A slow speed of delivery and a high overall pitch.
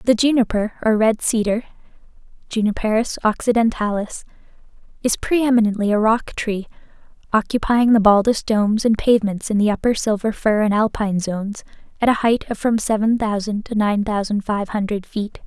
No: average, 150 wpm; high, 215 Hz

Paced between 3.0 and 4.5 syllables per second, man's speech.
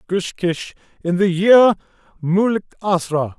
Yes: 3.7 syllables/s; male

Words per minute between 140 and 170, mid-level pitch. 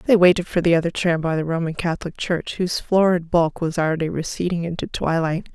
No: fast, 205 wpm; medium, 170 Hz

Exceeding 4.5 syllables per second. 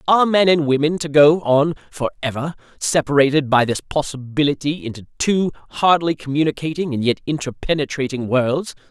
Yes: 5.5 syllables/s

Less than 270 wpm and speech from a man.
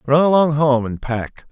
Yes: average, 200 wpm; male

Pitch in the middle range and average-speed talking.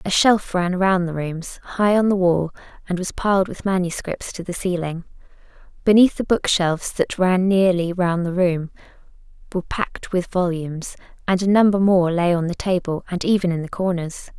Yes: medium, 180 Hz; average, 190 wpm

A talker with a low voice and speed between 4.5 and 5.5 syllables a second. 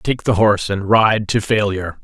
Yes: low, 105 Hz; 5.1 syllables/s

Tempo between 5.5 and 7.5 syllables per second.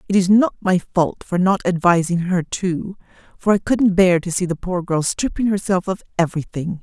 No: 5.1 syllables/s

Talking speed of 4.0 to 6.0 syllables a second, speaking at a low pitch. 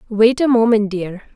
No: 4.7 syllables/s; high, 220 Hz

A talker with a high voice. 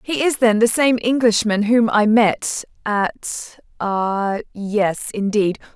Yes: high, 220 Hz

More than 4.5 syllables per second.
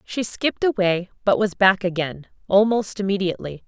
Yes: 5.3 syllables/s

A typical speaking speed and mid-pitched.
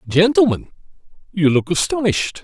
No: slow, 100 wpm; medium, 170 Hz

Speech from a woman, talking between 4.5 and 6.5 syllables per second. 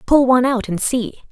Yes: female; 5.7 syllables/s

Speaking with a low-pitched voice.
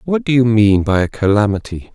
Yes: low, 110 Hz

